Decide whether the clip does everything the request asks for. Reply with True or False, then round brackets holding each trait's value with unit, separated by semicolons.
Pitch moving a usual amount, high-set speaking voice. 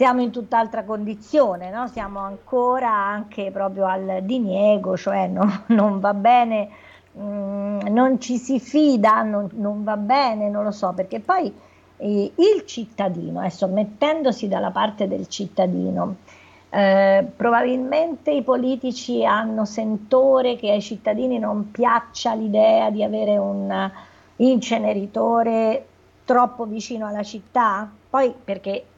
True (3.6 semitones; 215 Hz)